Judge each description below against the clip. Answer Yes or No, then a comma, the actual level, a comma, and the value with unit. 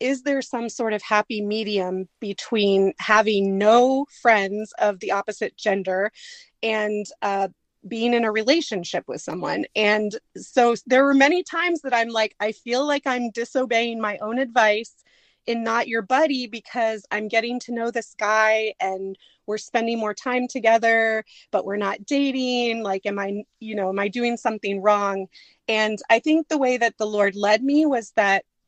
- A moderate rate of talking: Yes, average, 175 wpm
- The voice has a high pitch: Yes, high, 220 Hz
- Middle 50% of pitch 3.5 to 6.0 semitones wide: No, average, 2.8 semitones